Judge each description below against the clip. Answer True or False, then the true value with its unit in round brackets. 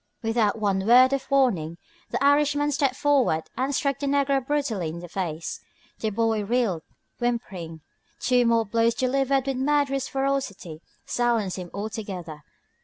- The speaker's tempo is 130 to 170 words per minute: True (145 wpm)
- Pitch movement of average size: False (5.7 semitones)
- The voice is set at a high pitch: True (240 Hz)